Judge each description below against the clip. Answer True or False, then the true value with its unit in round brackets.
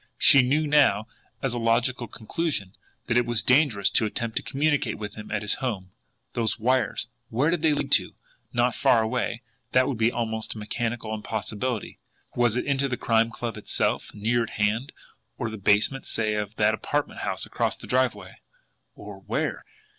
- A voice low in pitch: True (115 Hz)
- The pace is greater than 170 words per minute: True (180 wpm)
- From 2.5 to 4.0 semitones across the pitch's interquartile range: True (3.0 semitones)